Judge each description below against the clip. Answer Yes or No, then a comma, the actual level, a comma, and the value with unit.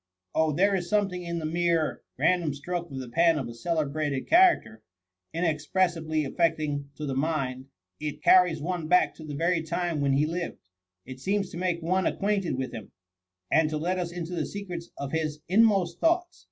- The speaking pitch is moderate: Yes, medium, 165 Hz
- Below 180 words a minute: No, average, 200 wpm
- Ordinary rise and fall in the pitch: Yes, average, 3.2 semitones